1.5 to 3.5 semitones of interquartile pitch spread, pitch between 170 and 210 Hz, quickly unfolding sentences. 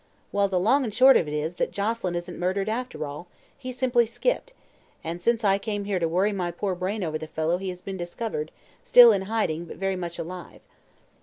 No: average, 4.2 semitones; high, 190 Hz; fast, 220 wpm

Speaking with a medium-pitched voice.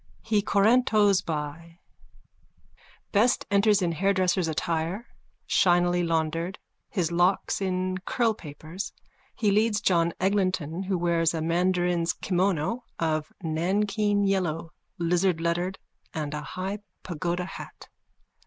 Yes: medium, 180 Hz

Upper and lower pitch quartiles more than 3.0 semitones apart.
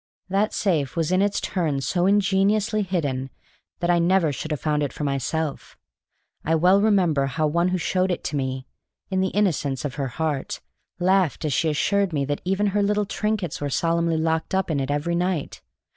Yes: average, 4.6 semitones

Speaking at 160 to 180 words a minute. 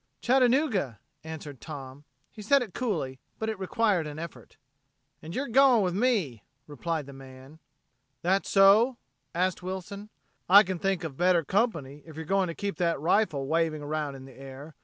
Yes: average, 170 wpm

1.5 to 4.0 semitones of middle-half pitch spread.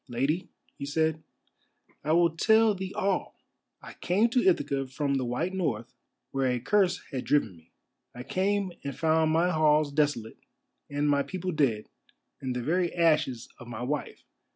No: wide, 5.4 semitones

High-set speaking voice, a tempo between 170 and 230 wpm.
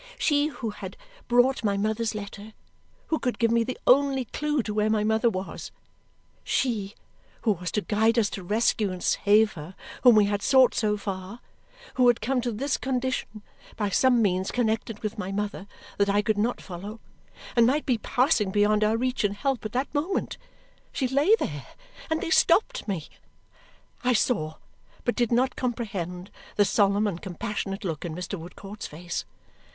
Yes: high, 215 Hz; average, 175 wpm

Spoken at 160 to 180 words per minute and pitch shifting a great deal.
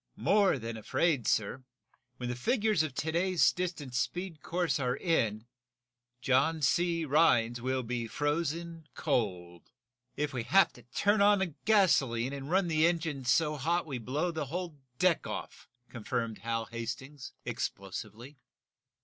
No: average, 140 wpm; wide, 5.8 semitones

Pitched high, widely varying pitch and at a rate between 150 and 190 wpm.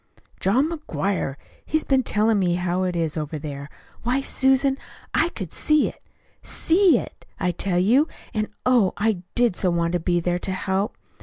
Yes: high, 195 Hz; wide, 6.8 semitones; average, 175 wpm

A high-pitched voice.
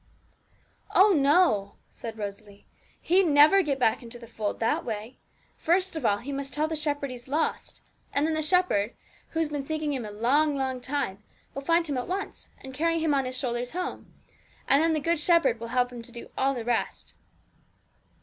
Yes: very high, 275 Hz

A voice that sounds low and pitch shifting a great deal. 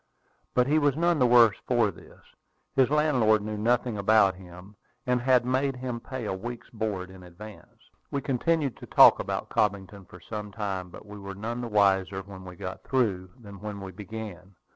No: low, 105 Hz; average, 4.3 semitones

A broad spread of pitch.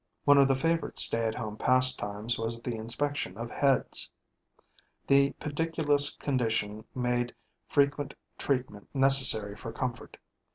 No: average, 3.8 semitones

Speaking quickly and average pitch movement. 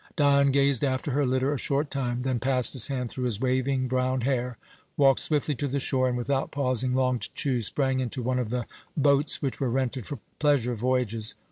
No: fast, 210 wpm; narrow, 1.9 semitones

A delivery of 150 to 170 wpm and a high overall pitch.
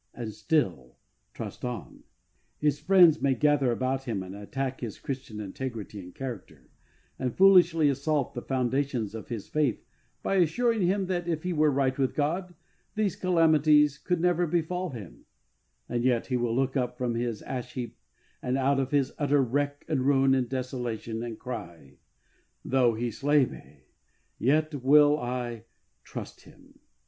No: average, 160 wpm; low, 135 Hz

